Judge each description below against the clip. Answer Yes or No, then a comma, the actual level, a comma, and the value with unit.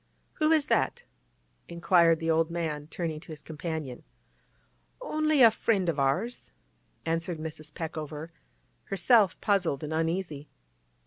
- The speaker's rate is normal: No, slow, 125 wpm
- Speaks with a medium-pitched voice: Yes, medium, 165 Hz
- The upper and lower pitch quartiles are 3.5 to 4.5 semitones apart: Yes, average, 3.8 semitones